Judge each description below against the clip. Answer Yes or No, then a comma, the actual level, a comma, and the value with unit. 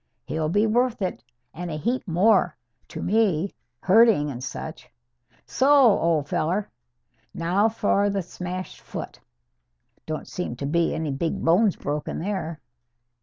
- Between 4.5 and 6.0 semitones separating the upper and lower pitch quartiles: Yes, average, 4.8 semitones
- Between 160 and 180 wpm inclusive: No, slow, 135 wpm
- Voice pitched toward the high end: No, medium, 180 Hz